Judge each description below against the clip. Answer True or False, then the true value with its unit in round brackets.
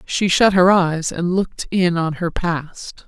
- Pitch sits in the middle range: True (175 Hz)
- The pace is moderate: True (195 wpm)